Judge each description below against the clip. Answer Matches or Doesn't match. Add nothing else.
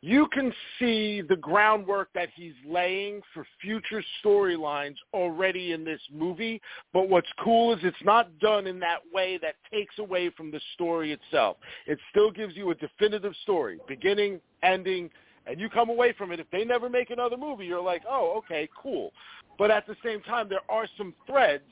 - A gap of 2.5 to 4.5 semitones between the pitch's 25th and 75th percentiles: Matches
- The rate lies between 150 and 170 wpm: Doesn't match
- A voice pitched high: Matches